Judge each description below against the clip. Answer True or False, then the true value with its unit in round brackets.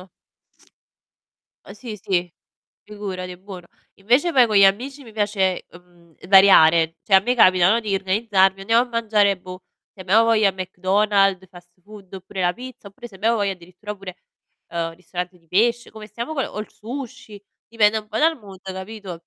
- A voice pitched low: False (200 Hz)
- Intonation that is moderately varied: True (3.2 semitones)